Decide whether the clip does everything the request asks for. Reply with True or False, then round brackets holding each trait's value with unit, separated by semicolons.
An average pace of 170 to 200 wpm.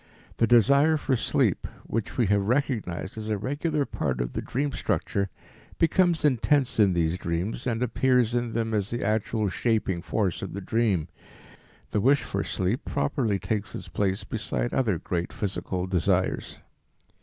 False (160 wpm)